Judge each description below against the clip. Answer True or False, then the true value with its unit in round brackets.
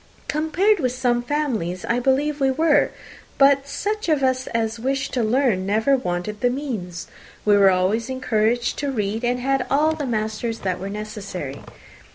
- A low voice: False (245 Hz)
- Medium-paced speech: True (170 wpm)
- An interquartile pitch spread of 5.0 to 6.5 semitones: False (4.6 semitones)